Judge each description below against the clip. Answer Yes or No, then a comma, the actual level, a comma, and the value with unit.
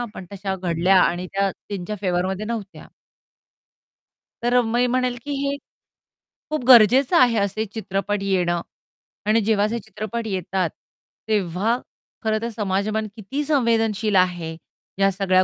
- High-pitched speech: Yes, high, 210 Hz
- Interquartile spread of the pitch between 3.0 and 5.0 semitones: Yes, average, 3.5 semitones